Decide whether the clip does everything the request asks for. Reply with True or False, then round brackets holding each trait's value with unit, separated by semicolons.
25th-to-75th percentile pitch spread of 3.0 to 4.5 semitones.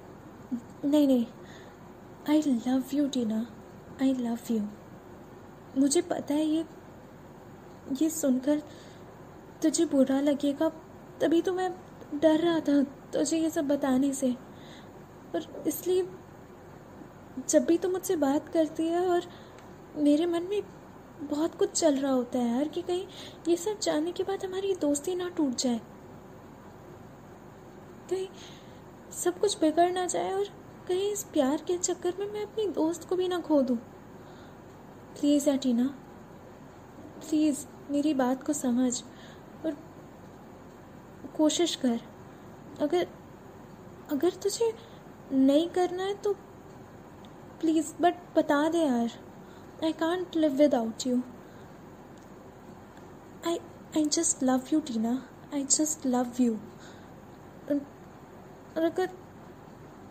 True (4.2 semitones)